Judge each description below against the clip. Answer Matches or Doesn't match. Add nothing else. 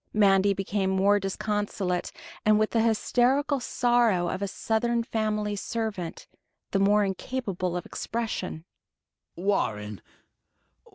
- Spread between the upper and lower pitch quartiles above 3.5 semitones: Doesn't match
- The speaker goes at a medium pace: Doesn't match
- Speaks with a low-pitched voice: Doesn't match